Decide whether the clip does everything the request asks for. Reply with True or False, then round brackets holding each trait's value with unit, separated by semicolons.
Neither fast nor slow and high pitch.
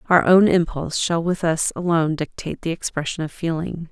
False (185 wpm; 165 Hz)